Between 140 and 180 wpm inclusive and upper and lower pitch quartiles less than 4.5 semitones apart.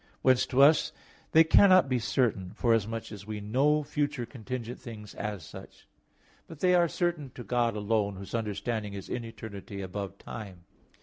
No: average, 165 wpm; average, 4.8 semitones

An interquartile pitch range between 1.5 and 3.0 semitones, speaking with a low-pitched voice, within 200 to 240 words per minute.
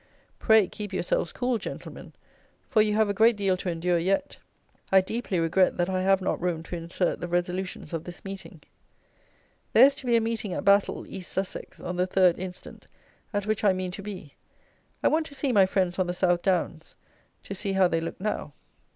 No: average, 2.7 semitones; high, 190 Hz; fast, 205 wpm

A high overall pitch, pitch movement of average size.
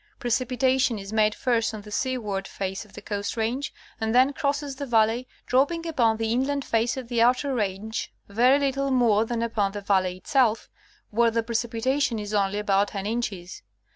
Yes: high, 230 Hz; average, 3.6 semitones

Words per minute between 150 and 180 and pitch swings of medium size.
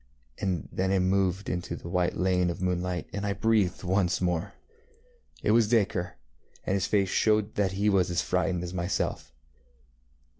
No: average, 175 wpm; narrow, 2.0 semitones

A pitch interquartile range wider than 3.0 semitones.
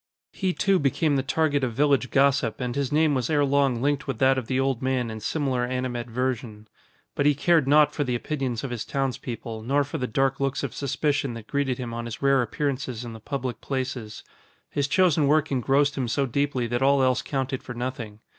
No: narrow, 2.6 semitones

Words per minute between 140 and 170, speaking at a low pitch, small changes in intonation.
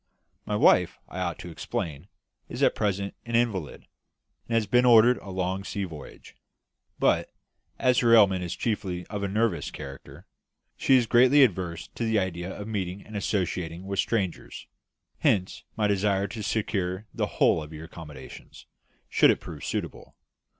No: average, 165 wpm; low, 100 Hz; average, 3.7 semitones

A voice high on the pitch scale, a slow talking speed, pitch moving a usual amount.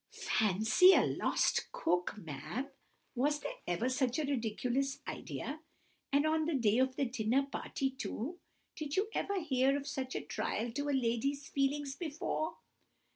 No: very high, 275 Hz; average, 155 wpm; average, 3.5 semitones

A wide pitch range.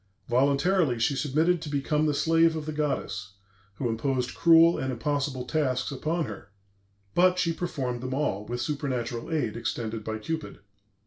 No: average, 4.7 semitones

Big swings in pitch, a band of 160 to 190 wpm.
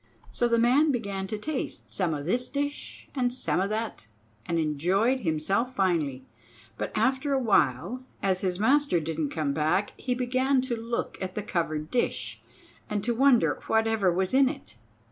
Yes: wide, 6.5 semitones; average, 170 wpm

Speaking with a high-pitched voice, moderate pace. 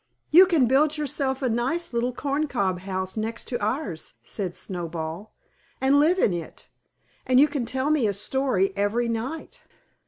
Yes: high, 240 Hz; average, 160 wpm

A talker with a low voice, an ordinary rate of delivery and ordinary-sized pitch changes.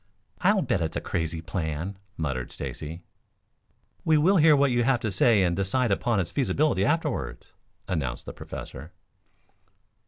No: low, 100 Hz; average, 150 wpm; wide, 8.7 semitones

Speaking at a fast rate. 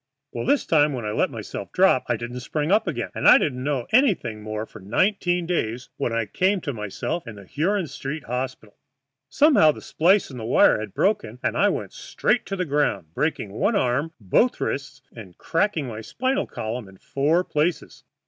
No: average, 195 wpm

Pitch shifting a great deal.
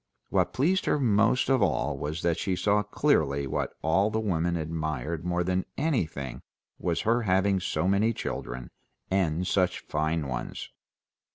No: average, 4.8 semitones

